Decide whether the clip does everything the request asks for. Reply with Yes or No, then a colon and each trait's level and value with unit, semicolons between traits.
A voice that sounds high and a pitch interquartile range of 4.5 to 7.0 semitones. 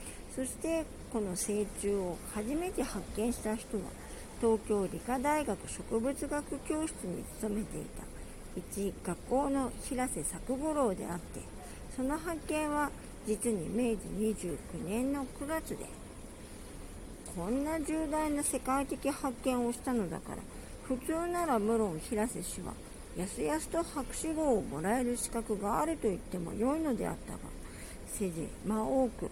Yes: very high, 250 Hz; wide, 5.5 semitones